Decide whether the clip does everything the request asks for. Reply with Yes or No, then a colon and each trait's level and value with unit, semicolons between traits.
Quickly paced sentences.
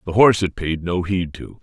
Yes: fast, 260 wpm